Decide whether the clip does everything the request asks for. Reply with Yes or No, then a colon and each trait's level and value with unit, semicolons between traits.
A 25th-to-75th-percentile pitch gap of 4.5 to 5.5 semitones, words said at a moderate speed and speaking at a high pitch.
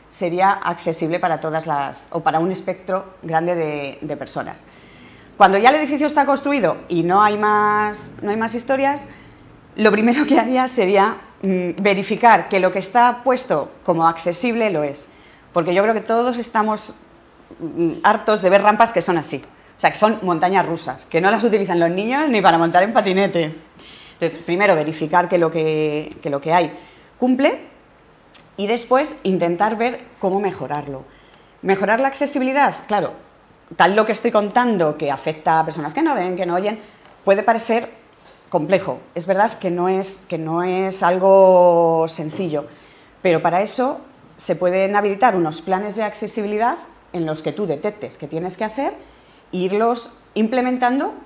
Yes: average, 4.9 semitones; average, 165 wpm; high, 195 Hz